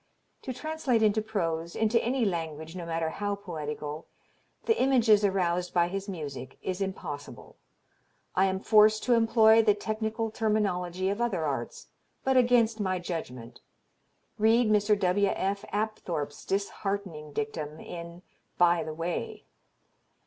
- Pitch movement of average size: Yes, average, 4.4 semitones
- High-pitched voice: Yes, high, 195 Hz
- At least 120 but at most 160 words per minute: Yes, slow, 135 wpm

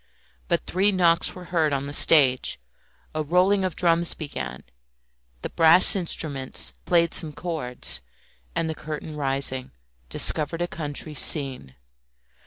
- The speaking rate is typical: No, slow, 130 wpm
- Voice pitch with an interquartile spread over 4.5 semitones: No, average, 3.5 semitones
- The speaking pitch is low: No, medium, 155 Hz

